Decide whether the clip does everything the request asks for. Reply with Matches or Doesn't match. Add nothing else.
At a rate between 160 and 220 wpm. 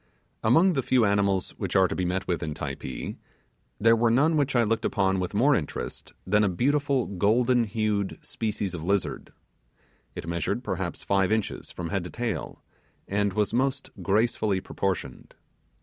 Matches